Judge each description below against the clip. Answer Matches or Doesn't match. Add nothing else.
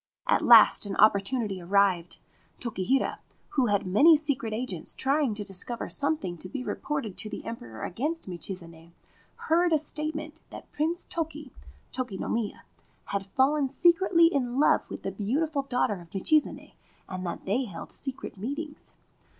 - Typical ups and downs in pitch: Doesn't match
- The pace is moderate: Matches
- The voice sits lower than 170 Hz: Doesn't match